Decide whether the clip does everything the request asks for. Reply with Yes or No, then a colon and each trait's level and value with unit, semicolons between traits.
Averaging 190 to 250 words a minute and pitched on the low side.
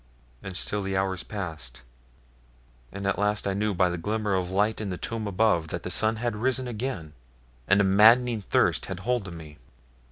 Yes: average, 195 wpm; low, 100 Hz